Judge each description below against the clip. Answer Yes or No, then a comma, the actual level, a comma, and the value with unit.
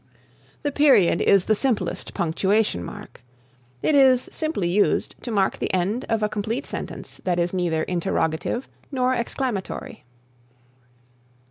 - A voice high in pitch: Yes, high, 210 Hz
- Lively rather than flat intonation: Yes, wide, 6.2 semitones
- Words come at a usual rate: No, slow, 130 wpm